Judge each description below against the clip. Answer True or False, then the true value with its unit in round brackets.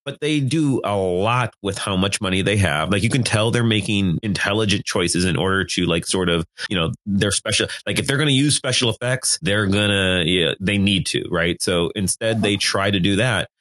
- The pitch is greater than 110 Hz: False (100 Hz)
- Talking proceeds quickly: True (230 wpm)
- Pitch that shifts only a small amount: False (3.2 semitones)